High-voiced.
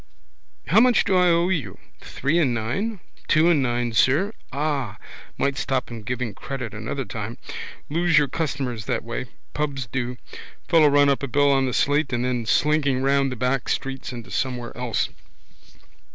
No: low, 135 Hz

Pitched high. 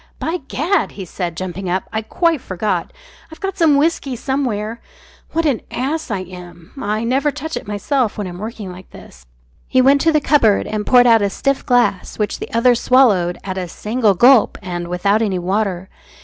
Yes: high, 220 Hz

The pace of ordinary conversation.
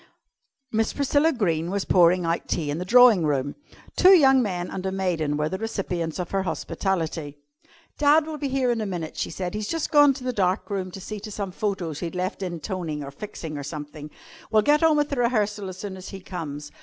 No: fast, 225 wpm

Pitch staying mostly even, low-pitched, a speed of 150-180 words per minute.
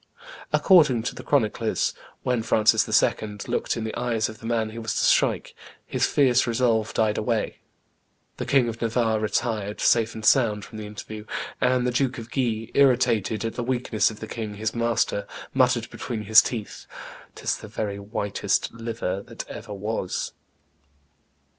Yes: narrow, 2.0 semitones; low, 115 Hz; average, 165 wpm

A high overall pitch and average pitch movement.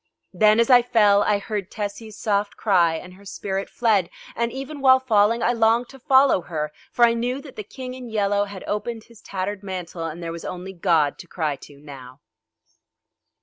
Yes: high, 205 Hz; average, 4.4 semitones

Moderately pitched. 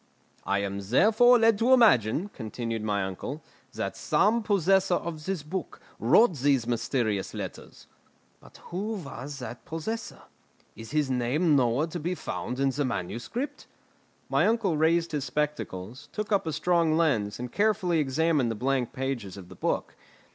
Yes: medium, 150 Hz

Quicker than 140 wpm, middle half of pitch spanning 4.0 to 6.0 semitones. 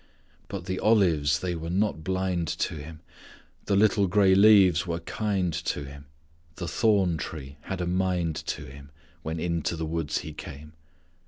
No: average, 165 wpm; average, 3.3 semitones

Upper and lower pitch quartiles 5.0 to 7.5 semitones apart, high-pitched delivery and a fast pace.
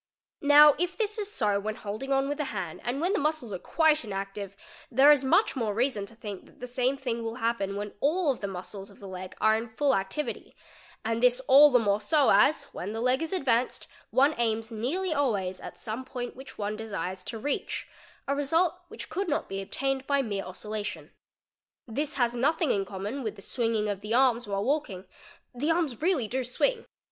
Yes: wide, 5.6 semitones; high, 245 Hz; fast, 210 wpm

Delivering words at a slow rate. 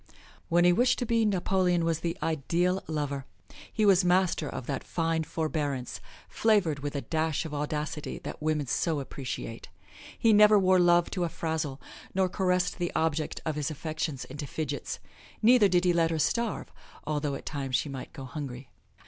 No: average, 175 wpm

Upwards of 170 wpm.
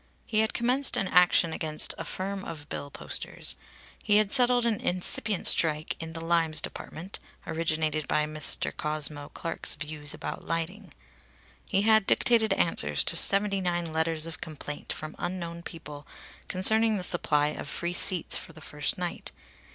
No: average, 160 wpm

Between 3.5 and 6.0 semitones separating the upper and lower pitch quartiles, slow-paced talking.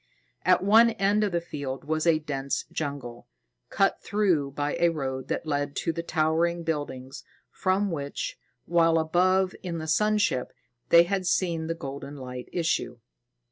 No: average, 4.3 semitones; average, 160 wpm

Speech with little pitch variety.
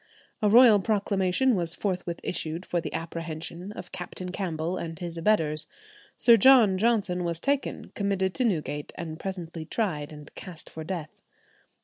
No: average, 3.7 semitones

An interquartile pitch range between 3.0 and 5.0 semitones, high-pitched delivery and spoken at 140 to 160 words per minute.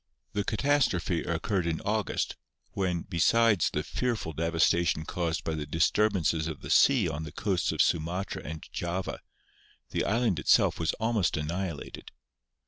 No: average, 4.2 semitones; very low, 85 Hz; average, 150 wpm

